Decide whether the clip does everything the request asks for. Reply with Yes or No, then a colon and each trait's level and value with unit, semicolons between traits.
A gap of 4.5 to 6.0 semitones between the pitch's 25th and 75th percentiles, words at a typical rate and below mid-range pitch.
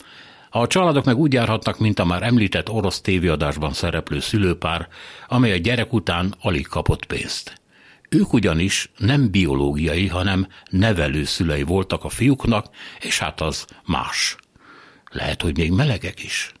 Yes: average, 5.1 semitones; average, 140 wpm; very low, 95 Hz